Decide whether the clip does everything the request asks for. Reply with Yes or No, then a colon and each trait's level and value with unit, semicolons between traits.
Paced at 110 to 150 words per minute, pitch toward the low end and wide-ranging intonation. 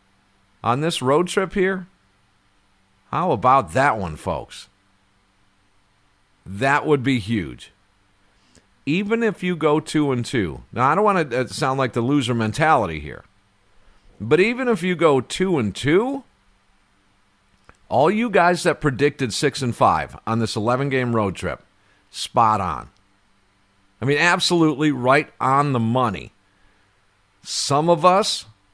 Yes: average, 140 wpm; low, 120 Hz; wide, 7.4 semitones